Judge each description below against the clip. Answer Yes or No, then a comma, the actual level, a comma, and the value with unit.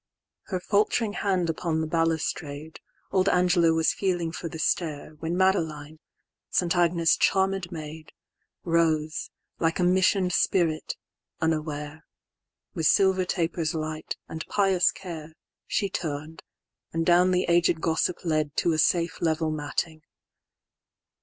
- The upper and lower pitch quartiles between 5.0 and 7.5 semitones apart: No, narrow, 2.4 semitones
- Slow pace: Yes, slow, 110 wpm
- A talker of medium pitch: Yes, medium, 165 Hz